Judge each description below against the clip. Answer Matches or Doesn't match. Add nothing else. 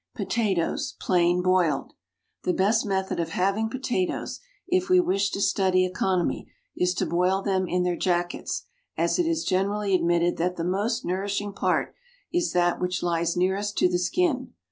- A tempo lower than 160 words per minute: Doesn't match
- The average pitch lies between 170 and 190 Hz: Matches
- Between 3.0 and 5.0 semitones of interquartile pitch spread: Doesn't match